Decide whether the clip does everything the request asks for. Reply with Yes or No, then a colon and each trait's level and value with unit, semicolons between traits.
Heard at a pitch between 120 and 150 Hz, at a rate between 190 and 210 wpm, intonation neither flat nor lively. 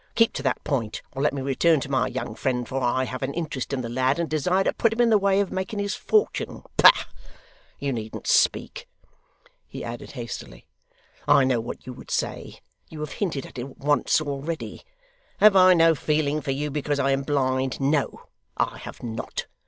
Yes: medium, 140 Hz; average, 200 wpm; average, 4.1 semitones